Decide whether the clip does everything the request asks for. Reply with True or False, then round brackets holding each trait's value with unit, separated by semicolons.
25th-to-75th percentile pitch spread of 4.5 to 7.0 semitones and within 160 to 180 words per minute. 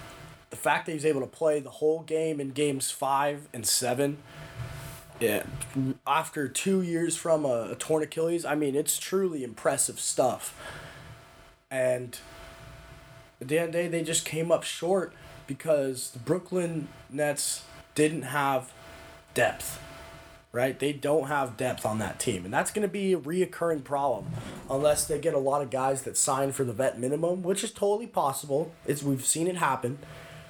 False (3.7 semitones; 170 wpm)